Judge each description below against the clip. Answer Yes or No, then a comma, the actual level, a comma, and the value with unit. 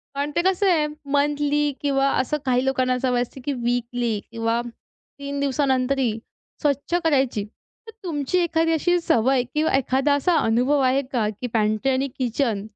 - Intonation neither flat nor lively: Yes, average, 3.1 semitones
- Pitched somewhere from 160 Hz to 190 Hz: No, very high, 270 Hz